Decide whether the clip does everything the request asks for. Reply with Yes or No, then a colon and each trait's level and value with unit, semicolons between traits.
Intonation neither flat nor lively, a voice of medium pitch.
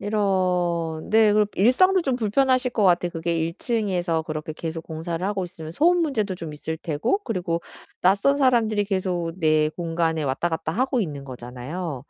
Yes: average, 5.0 semitones; medium, 175 Hz